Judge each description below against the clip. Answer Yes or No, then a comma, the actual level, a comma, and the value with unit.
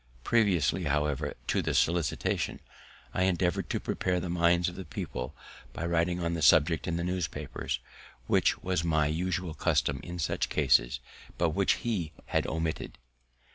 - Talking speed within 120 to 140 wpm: No, average, 155 wpm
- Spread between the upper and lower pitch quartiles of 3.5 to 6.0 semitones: No, narrow, 2.6 semitones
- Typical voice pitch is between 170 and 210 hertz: No, very low, 85 Hz